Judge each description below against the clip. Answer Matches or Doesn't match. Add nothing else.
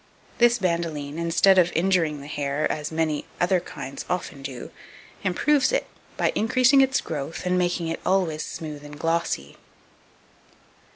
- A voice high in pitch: Doesn't match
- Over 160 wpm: Doesn't match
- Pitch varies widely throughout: Doesn't match